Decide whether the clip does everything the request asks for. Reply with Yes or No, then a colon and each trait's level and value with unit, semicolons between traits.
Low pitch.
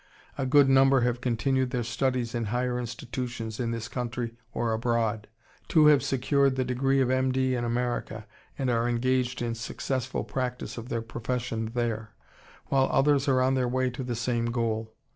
Yes: low, 125 Hz